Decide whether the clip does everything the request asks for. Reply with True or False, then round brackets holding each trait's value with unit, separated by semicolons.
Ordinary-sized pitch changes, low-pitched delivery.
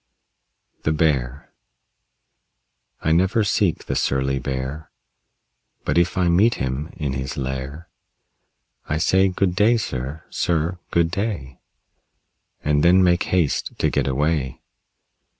True (4.9 semitones; 80 Hz)